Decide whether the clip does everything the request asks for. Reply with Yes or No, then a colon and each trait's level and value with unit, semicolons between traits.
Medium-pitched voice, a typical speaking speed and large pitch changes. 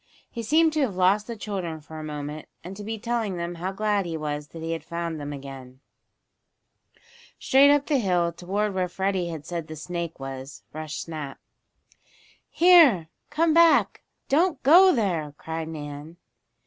Yes: medium, 175 Hz; average, 170 wpm; wide, 5.9 semitones